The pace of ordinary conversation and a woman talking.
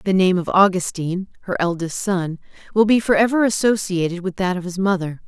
Yes: average, 195 wpm; female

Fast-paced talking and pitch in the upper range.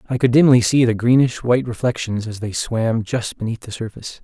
No: fast, 215 wpm; low, 115 Hz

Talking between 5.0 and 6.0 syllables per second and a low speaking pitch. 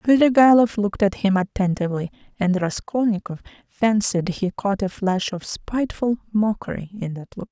No: 5.1 syllables/s; high, 205 Hz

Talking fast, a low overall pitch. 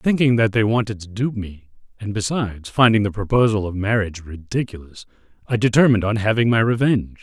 No: average, 175 wpm; low, 110 Hz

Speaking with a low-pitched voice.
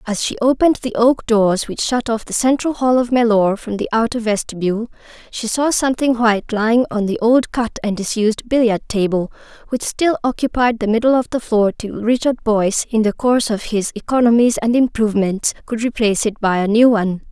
No: high, 230 Hz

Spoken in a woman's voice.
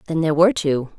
Yes: female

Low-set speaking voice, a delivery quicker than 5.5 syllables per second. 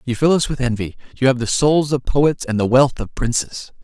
No: low, 130 Hz; 5.2 syllables/s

